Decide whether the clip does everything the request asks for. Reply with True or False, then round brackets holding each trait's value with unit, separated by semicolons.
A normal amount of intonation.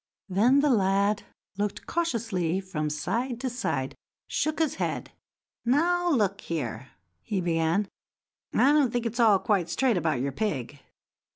False (6.9 semitones)